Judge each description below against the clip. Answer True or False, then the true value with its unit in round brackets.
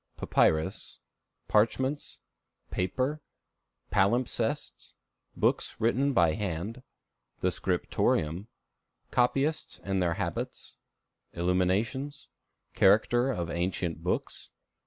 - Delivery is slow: True (75 wpm)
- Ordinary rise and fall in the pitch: False (6.4 semitones)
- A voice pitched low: True (105 Hz)